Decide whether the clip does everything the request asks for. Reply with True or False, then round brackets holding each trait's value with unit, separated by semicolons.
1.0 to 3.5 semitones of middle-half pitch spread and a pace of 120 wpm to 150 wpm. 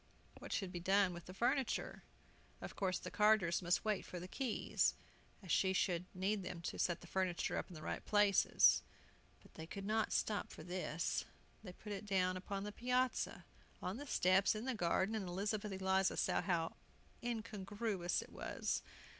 False (2.7 semitones; 180 wpm)